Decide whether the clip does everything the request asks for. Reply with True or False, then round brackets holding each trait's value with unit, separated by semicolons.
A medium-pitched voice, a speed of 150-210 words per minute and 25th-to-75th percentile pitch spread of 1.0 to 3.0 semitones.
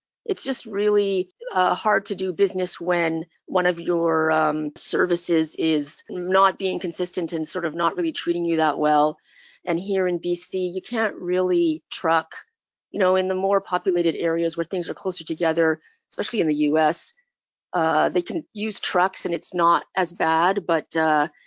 True (175 Hz; 175 wpm; 2.5 semitones)